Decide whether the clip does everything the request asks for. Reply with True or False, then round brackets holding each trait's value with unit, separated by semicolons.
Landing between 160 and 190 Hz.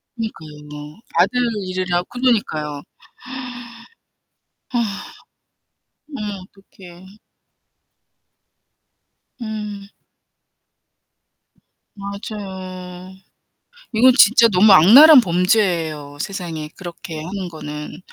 True (185 Hz)